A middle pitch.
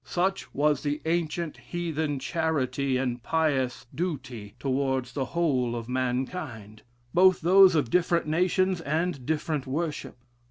Yes: medium, 150 Hz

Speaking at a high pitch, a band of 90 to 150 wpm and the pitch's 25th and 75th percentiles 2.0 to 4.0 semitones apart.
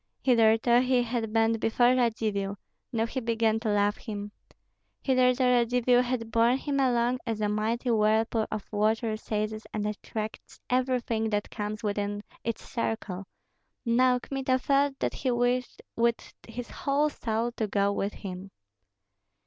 Yes: high, 230 Hz; average, 145 wpm; narrow, 2.6 semitones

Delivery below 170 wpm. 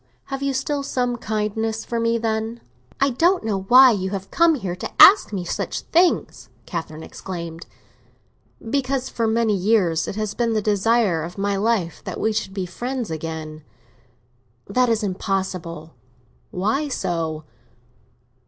Yes: average, 150 wpm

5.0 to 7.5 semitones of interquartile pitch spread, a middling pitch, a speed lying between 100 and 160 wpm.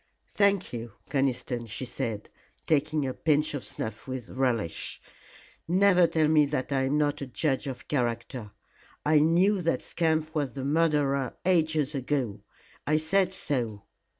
No: average, 3.7 semitones; medium, 145 Hz; average, 150 wpm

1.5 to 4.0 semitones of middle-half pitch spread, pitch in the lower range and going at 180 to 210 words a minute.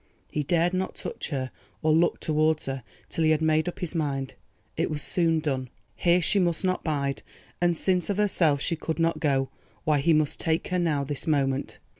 No: average, 3.3 semitones; medium, 155 Hz; average, 200 wpm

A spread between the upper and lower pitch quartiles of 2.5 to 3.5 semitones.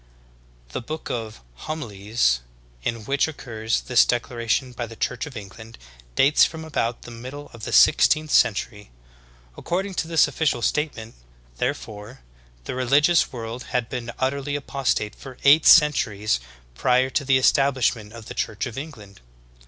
No: average, 4.2 semitones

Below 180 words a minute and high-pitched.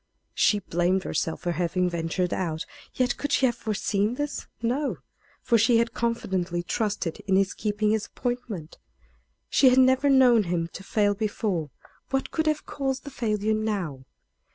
Yes: average, 160 wpm; high, 210 Hz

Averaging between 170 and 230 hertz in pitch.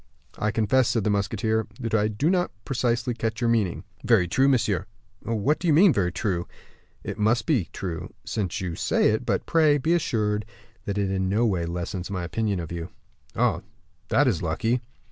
No: low, 110 Hz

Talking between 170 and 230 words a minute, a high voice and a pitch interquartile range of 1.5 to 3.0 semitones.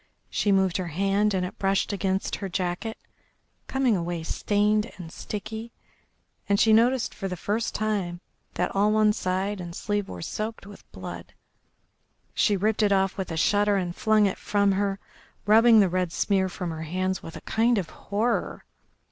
Yes: average, 175 wpm; high, 200 Hz; narrow, 2.5 semitones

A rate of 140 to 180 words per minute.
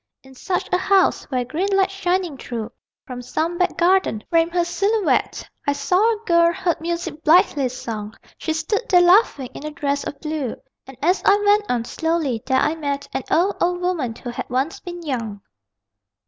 No: average, 190 wpm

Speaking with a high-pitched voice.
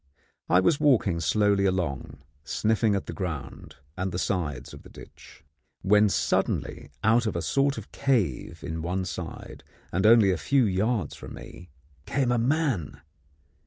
No: very low, 95 Hz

